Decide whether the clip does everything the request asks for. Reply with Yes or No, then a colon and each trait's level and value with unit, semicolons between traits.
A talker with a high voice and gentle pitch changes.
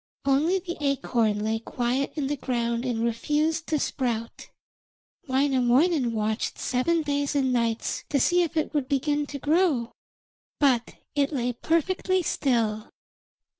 No: very high, 275 Hz; average, 4.2 semitones